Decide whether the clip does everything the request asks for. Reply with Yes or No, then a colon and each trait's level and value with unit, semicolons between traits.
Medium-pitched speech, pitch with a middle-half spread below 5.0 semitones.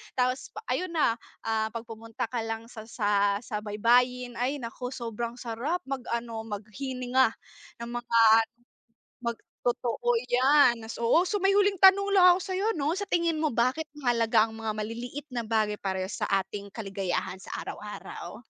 No: high, 240 Hz; average, 4.6 semitones